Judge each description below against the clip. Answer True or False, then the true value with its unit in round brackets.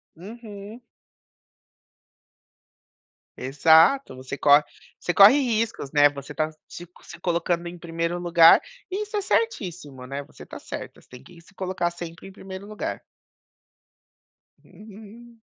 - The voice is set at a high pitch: False (175 Hz)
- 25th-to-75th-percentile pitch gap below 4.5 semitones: False (5.0 semitones)